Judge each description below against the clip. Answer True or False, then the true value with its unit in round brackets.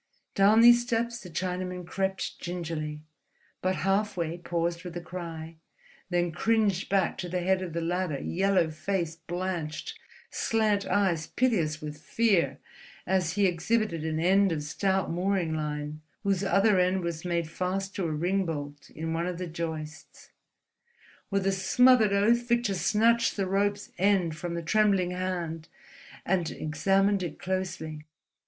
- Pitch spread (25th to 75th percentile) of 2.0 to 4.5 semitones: True (3.1 semitones)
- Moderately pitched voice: True (180 Hz)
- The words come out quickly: False (150 wpm)